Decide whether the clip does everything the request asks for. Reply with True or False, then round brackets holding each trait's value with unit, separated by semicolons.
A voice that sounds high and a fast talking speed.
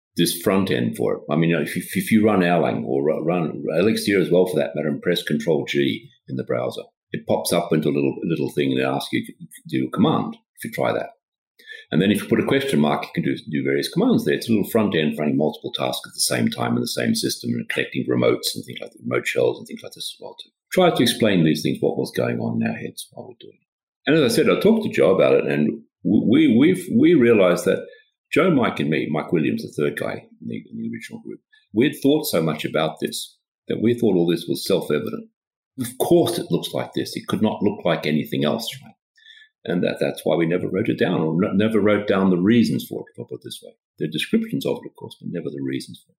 False (105 Hz; 275 wpm)